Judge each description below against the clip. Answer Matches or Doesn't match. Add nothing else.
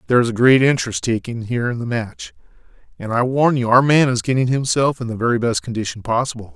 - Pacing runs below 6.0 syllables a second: Doesn't match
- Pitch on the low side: Matches